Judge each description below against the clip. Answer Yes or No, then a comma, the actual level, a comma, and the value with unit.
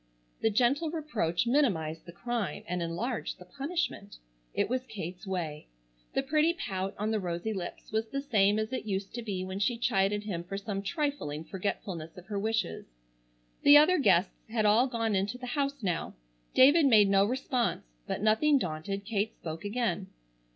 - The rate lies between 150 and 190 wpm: Yes, average, 175 wpm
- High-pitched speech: Yes, high, 210 Hz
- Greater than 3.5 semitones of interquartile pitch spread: Yes, average, 4.8 semitones